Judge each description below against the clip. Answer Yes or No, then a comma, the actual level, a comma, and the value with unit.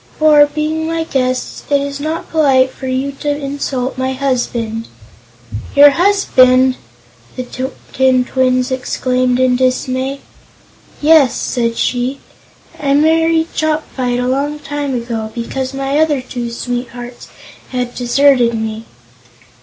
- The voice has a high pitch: Yes, very high, 260 Hz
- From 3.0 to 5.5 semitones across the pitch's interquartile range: No, narrow, 2.5 semitones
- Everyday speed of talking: No, slow, 120 wpm